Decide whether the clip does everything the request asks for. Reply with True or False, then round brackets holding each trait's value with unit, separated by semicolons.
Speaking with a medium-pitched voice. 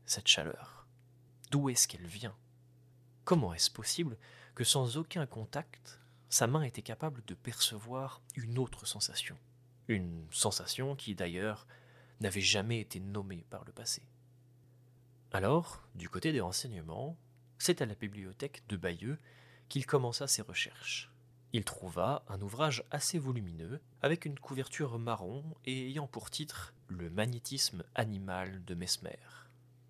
False (125 Hz)